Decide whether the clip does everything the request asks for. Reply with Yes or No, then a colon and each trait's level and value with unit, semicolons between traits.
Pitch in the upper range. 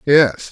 No: low, 135 Hz